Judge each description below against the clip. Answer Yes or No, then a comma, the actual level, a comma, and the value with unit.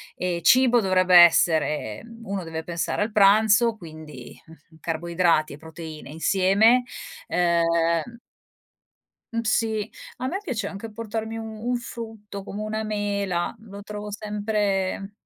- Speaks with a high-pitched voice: Yes, high, 200 Hz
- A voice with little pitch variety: No, average, 4.5 semitones